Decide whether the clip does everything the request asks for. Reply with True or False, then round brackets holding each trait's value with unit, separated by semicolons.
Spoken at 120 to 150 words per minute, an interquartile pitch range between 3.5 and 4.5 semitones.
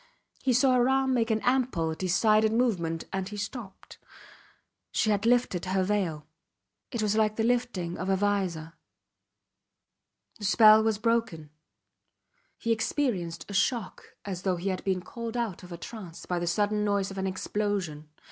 False (165 wpm; 3.9 semitones)